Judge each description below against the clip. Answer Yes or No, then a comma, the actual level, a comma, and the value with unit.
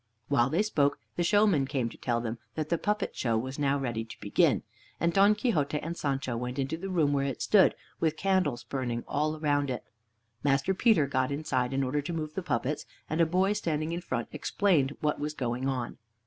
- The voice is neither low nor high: Yes, medium, 145 Hz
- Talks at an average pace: No, fast, 210 wpm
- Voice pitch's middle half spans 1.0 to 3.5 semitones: No, average, 4.5 semitones